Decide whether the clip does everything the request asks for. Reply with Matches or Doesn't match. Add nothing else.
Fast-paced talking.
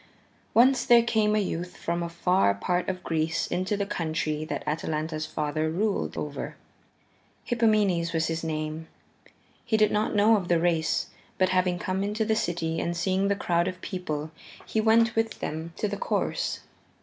Doesn't match